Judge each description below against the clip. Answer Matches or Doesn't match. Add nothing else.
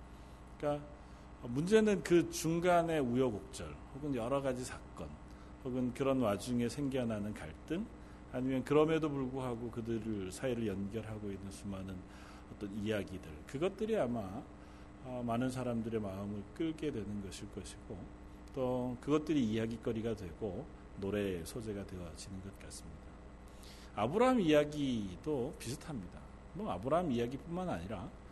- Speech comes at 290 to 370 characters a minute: Matches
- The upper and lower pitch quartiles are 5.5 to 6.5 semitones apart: Doesn't match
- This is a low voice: Matches